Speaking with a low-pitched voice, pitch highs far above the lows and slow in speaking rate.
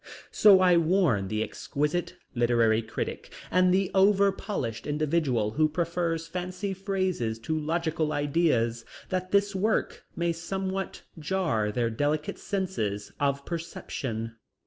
No: medium, 165 Hz; wide, 7.5 semitones; slow, 125 wpm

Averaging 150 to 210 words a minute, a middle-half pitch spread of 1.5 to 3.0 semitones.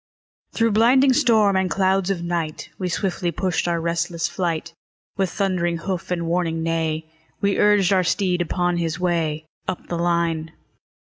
Yes: average, 155 wpm; narrow, 2.4 semitones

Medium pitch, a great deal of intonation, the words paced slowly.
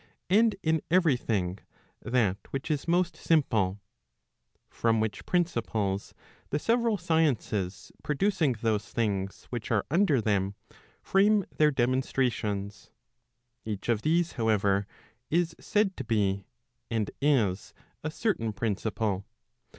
No: low, 120 Hz; wide, 8.0 semitones; slow, 120 wpm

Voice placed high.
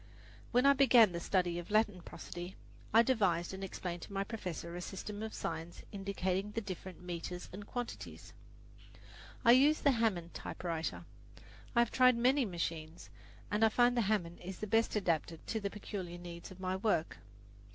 Yes: high, 195 Hz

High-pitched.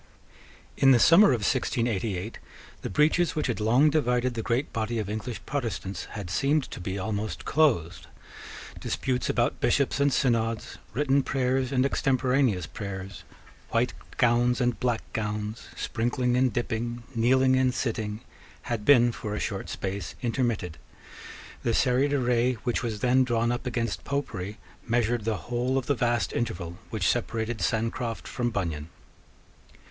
No: low, 120 Hz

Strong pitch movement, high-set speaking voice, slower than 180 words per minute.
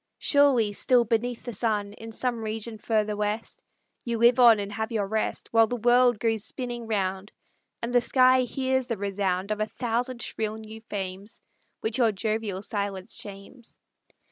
No: narrow, 2.6 semitones; high, 220 Hz; average, 170 wpm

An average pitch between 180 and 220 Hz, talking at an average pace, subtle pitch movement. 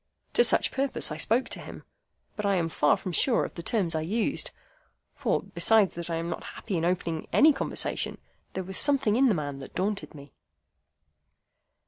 No: medium, 185 Hz; average, 190 wpm; wide, 5.6 semitones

